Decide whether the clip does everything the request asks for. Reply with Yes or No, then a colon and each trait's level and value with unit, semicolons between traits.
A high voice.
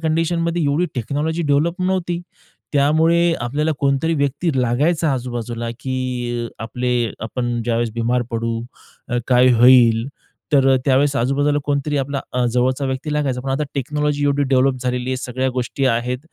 No: low, 135 Hz